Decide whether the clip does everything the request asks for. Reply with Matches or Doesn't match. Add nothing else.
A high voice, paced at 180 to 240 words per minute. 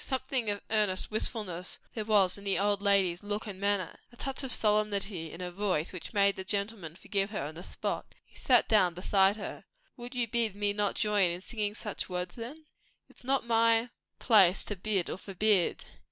Matches